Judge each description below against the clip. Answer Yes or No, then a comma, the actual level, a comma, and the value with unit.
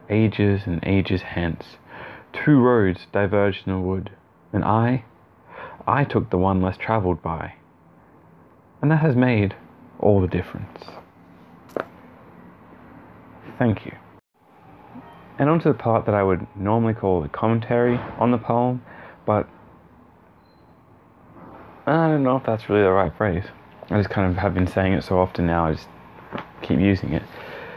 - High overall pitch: No, low, 100 Hz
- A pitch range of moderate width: Yes, average, 4.2 semitones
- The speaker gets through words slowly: No, average, 150 wpm